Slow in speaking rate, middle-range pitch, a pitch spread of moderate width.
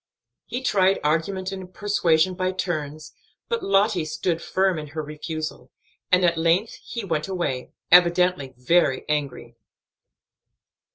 Yes: slow, 125 wpm; medium, 175 Hz; average, 3.5 semitones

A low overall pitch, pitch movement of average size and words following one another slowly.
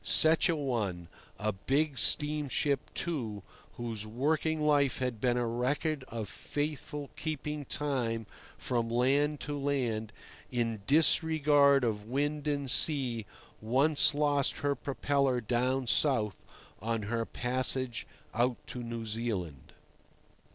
Yes: low, 130 Hz; average, 4.1 semitones; slow, 120 wpm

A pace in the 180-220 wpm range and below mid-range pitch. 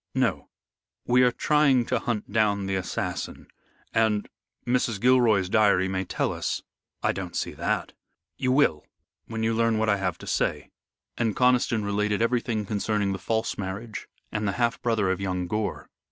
No: average, 170 wpm; low, 110 Hz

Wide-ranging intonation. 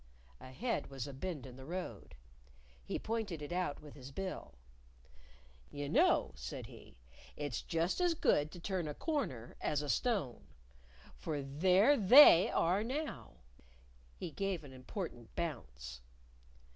Yes: wide, 6.4 semitones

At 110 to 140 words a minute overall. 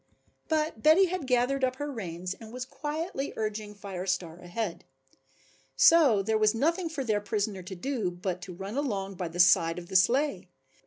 No: average, 180 wpm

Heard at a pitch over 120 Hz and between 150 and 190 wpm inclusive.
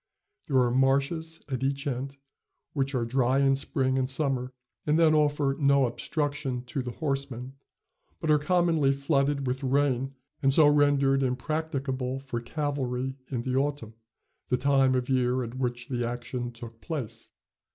Yes: low, 135 Hz; average, 155 wpm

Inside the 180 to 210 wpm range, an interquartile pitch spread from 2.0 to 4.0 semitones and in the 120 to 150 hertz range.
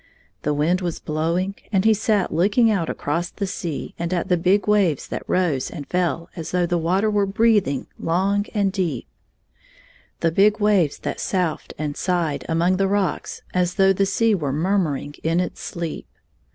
No: average, 185 wpm; average, 3.4 semitones; medium, 180 Hz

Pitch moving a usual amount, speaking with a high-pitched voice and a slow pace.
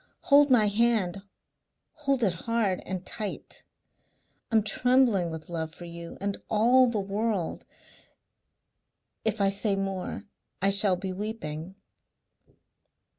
Yes: average, 3.7 semitones; high, 200 Hz; slow, 120 wpm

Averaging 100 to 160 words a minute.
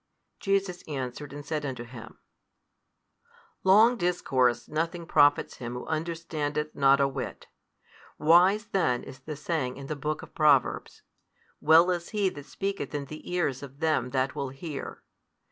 Yes: average, 150 wpm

